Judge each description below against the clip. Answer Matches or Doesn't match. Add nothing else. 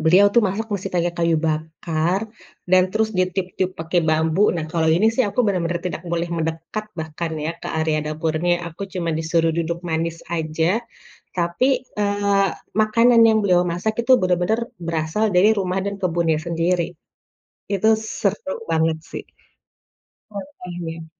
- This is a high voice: Doesn't match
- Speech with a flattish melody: Doesn't match